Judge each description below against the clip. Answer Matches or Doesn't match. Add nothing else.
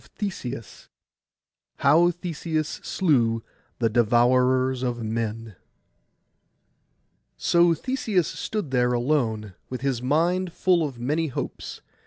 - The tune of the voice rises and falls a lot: Matches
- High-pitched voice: Doesn't match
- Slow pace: Matches